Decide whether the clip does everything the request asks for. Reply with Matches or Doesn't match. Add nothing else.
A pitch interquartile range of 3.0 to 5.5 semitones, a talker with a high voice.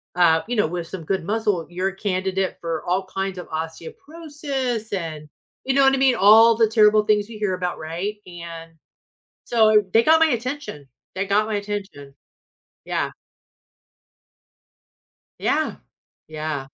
Matches